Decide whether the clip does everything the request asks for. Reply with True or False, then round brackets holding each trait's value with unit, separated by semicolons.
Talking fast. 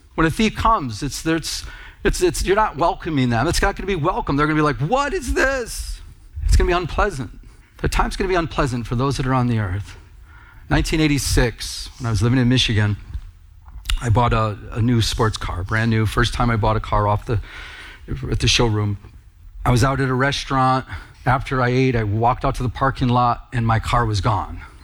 True (220 wpm)